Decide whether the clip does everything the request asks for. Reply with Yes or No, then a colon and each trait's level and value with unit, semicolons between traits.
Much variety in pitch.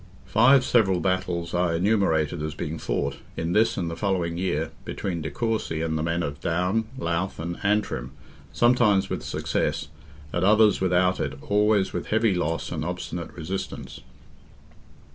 No: average, 3.8 semitones